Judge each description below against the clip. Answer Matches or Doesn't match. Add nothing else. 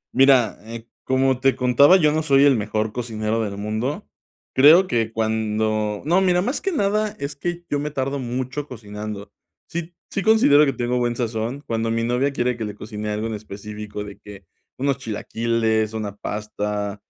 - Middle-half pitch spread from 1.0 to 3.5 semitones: Doesn't match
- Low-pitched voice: Matches